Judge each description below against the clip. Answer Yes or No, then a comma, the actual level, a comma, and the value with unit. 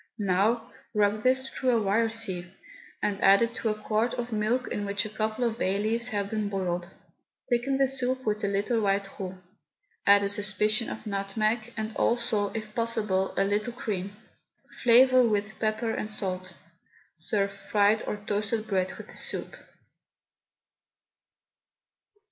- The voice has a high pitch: Yes, high, 215 Hz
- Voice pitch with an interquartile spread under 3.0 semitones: Yes, narrow, 2.5 semitones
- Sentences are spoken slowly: No, average, 155 wpm